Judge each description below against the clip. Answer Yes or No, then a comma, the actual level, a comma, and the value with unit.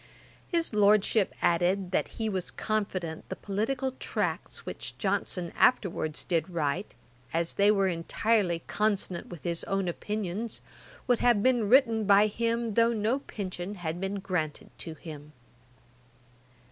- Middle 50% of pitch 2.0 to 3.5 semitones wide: No, average, 4.1 semitones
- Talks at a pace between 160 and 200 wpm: No, slow, 135 wpm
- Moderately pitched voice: No, high, 200 Hz